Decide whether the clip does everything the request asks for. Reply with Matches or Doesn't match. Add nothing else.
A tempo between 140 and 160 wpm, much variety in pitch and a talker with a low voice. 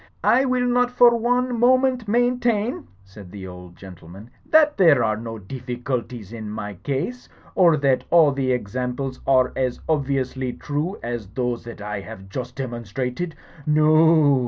Matches